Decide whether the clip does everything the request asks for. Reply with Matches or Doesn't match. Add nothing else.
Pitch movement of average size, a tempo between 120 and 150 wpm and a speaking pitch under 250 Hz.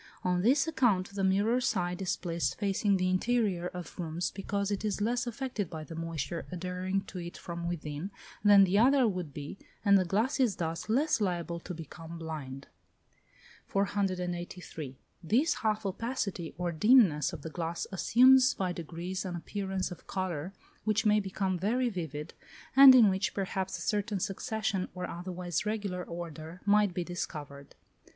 Doesn't match